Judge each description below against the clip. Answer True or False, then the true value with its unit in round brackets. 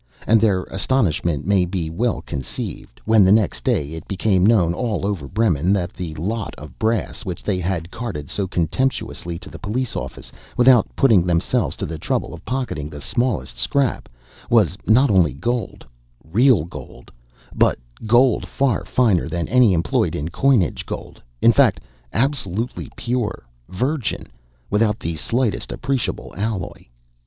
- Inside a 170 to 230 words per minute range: False (145 wpm)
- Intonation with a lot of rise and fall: True (5.9 semitones)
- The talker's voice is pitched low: True (100 Hz)